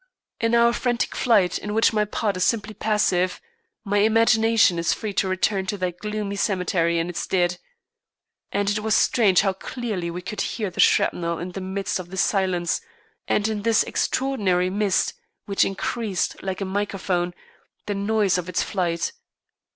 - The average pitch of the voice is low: No, high, 195 Hz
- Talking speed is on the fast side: No, average, 170 wpm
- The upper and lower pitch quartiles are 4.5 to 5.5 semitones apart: No, average, 2.9 semitones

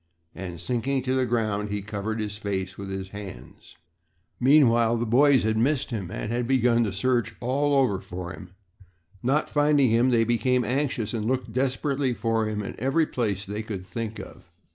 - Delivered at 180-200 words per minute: Yes, average, 185 wpm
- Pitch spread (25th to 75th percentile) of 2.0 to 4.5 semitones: Yes, average, 3.9 semitones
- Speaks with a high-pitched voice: No, low, 115 Hz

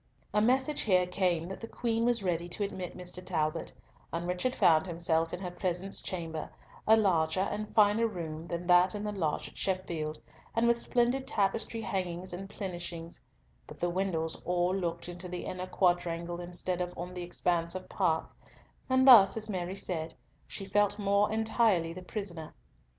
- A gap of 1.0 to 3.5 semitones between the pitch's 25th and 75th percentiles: Yes, average, 3.2 semitones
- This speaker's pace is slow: No, average, 175 wpm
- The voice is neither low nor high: Yes, medium, 180 Hz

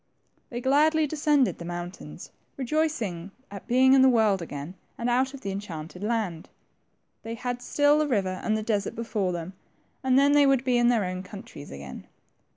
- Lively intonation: Yes, wide, 6.2 semitones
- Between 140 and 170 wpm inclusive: No, average, 180 wpm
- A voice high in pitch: Yes, high, 230 Hz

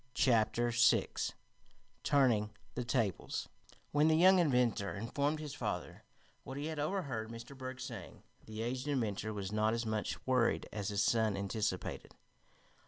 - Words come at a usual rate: Yes, average, 145 wpm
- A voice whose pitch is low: Yes, low, 120 Hz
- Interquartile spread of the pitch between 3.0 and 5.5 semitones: Yes, average, 4.1 semitones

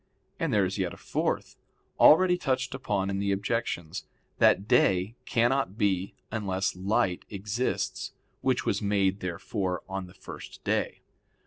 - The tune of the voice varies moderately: Yes, average, 3.4 semitones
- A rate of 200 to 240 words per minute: No, average, 140 wpm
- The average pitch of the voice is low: Yes, low, 100 Hz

